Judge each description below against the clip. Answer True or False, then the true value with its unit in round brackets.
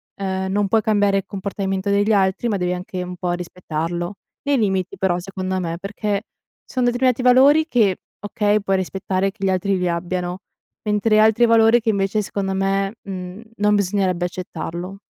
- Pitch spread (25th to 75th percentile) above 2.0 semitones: True (2.4 semitones)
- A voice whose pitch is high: True (195 Hz)